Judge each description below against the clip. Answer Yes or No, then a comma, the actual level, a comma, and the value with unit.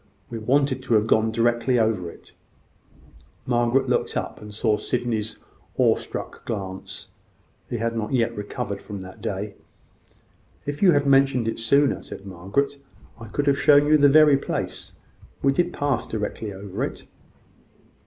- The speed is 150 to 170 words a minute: Yes, average, 155 wpm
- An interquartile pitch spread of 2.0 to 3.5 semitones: No, average, 4.6 semitones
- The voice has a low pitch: Yes, low, 115 Hz